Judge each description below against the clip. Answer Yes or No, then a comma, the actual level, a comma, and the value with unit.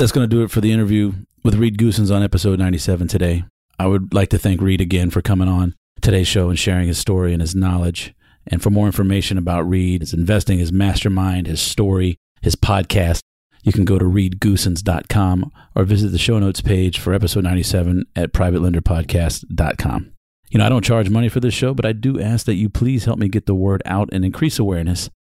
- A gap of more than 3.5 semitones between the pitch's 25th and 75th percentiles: No, average, 2.7 semitones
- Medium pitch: No, very low, 95 Hz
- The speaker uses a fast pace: Yes, fast, 210 wpm